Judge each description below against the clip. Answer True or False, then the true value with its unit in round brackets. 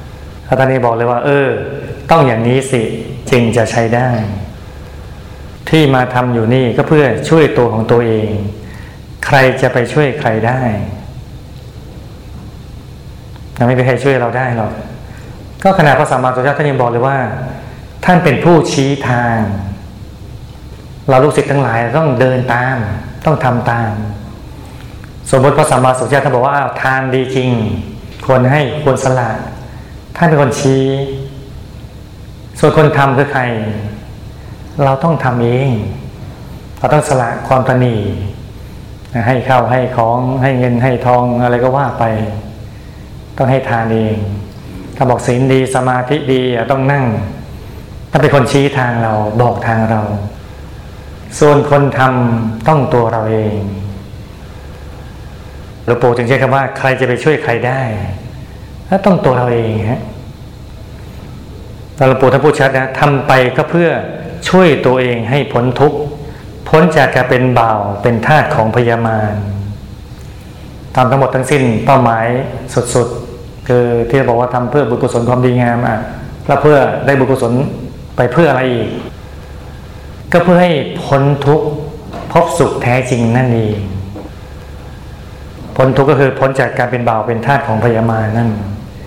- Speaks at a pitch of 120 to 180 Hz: True (125 Hz)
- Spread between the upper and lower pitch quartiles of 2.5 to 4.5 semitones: True (3.4 semitones)